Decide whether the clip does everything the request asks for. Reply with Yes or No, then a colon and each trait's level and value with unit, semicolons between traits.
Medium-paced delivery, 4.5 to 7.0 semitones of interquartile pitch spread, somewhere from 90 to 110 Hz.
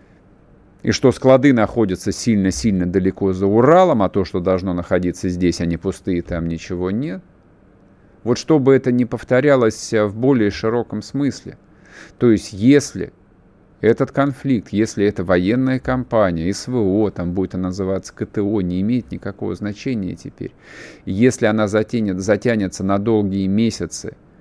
No: average, 140 wpm; average, 4.1 semitones; low, 105 Hz